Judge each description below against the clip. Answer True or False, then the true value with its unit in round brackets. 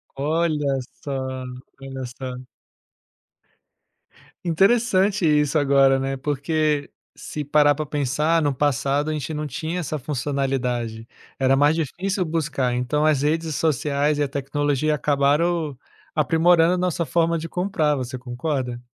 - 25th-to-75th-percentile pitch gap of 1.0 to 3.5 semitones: True (3.0 semitones)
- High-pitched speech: False (145 Hz)